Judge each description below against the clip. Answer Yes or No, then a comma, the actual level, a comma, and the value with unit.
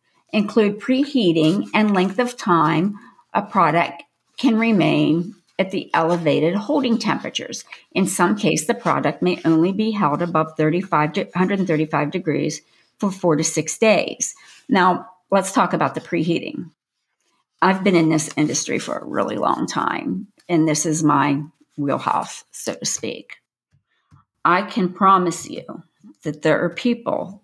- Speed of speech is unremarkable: Yes, average, 145 wpm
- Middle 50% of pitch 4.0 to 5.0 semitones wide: Yes, average, 4.7 semitones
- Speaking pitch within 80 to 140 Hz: No, medium, 175 Hz